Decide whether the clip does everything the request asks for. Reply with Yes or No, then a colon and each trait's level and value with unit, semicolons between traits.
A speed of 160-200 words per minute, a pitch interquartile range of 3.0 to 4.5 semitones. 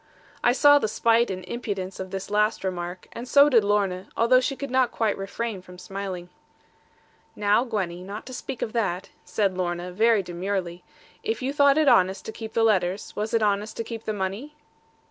Yes: average, 195 wpm; average, 3.9 semitones